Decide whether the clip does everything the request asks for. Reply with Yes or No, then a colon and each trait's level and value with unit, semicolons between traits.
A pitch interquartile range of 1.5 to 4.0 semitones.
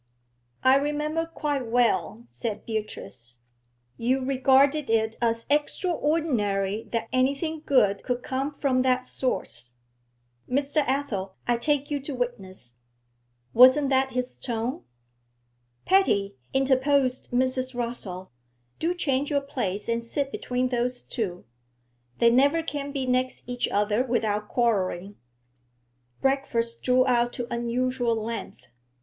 Yes: average, 3.3 semitones